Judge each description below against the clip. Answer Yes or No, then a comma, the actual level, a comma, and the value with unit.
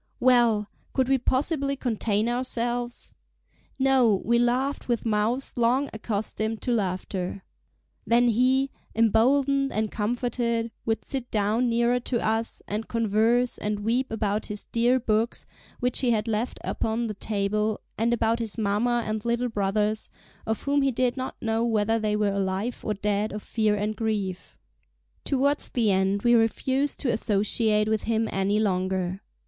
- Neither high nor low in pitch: No, high, 225 Hz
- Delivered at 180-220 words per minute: No, average, 155 wpm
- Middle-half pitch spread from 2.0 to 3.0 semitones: Yes, narrow, 2.6 semitones